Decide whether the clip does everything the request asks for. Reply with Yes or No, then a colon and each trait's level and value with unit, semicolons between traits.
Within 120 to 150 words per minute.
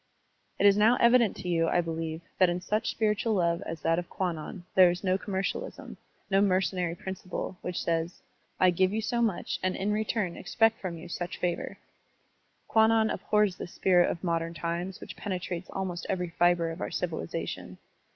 No: average, 180 wpm